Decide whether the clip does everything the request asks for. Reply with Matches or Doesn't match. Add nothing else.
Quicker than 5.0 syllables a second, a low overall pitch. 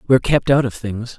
Matches